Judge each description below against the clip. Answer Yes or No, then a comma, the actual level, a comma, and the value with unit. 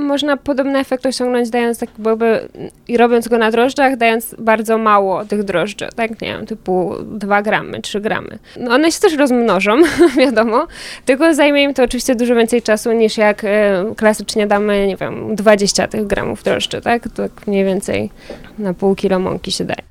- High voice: Yes, high, 225 Hz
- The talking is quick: Yes, fast, 180 wpm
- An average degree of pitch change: Yes, average, 3.2 semitones